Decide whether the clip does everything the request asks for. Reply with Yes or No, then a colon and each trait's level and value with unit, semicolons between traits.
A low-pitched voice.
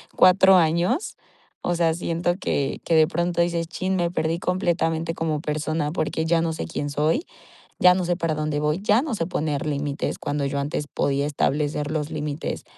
No: medium, 160 Hz